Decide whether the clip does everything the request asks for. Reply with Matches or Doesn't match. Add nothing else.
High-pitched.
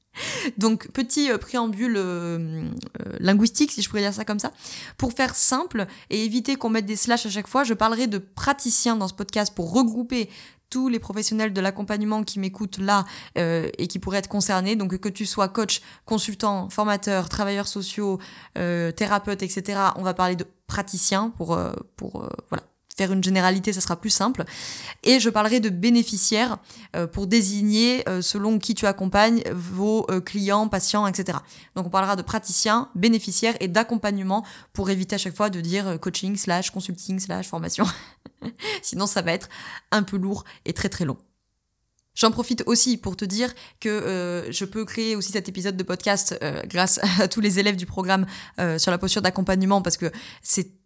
Matches